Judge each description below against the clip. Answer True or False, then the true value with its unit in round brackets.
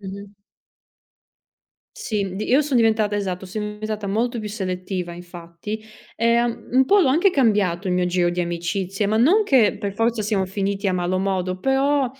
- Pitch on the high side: True (205 Hz)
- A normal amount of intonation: True (4.0 semitones)